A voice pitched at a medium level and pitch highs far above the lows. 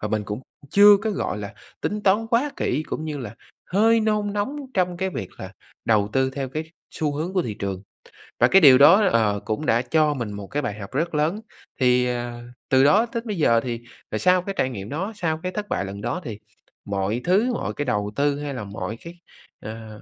Yes: medium, 145 Hz; wide, 9.0 semitones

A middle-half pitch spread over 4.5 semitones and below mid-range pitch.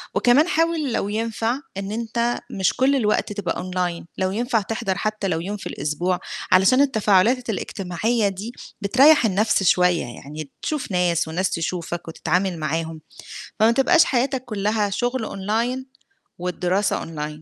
No: average, 4.9 semitones; high, 205 Hz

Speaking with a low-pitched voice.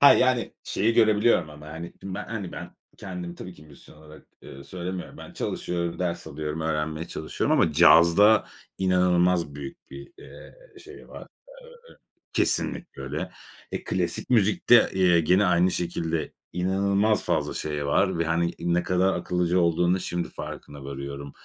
Yes: very low, 85 Hz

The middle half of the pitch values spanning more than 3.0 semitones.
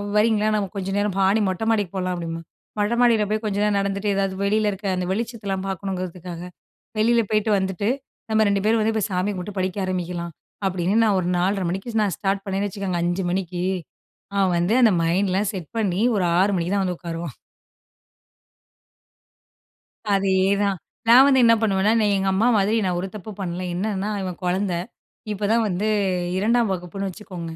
No: narrow, 2.4 semitones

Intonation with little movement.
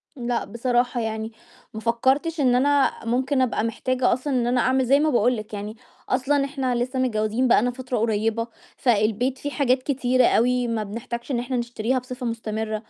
Yes: narrow, 2.2 semitones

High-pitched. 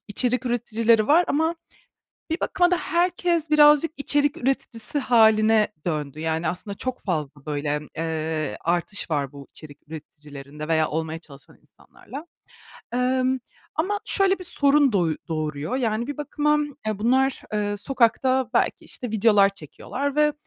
Yes: high, 225 Hz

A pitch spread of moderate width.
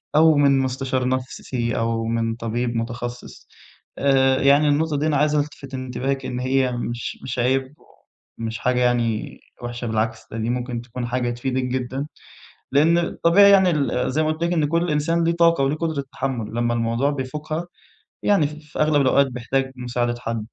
Yes: average, 3.6 semitones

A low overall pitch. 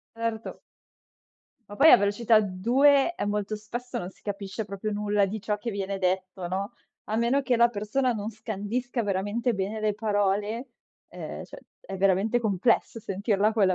No: high, 210 Hz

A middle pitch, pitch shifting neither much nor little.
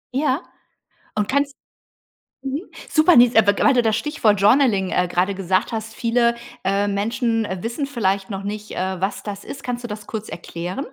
No: high, 220 Hz; average, 3.8 semitones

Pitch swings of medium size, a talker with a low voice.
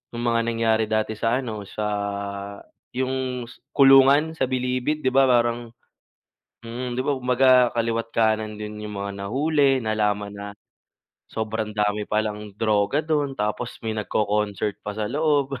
Yes: average, 3.5 semitones; low, 115 Hz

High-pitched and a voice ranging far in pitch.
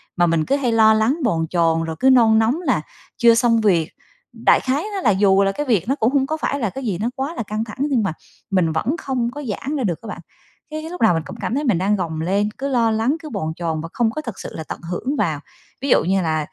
Yes: high, 220 Hz; wide, 6.3 semitones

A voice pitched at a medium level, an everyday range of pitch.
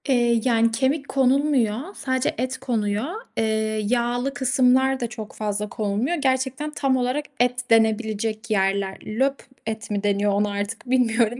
No: high, 240 Hz; average, 3.4 semitones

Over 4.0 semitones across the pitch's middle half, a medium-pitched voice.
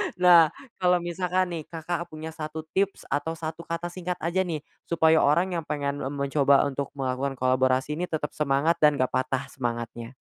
No: average, 3.7 semitones; medium, 155 Hz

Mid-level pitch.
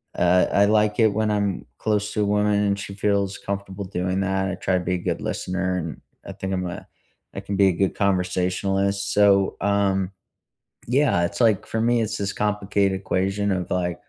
No: low, 100 Hz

